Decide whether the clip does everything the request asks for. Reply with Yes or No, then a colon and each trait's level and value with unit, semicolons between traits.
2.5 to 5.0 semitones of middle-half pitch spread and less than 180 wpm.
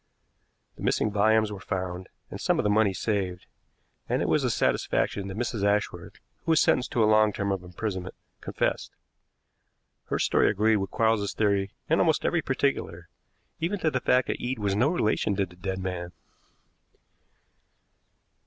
Yes: average, 2.9 semitones; average, 170 wpm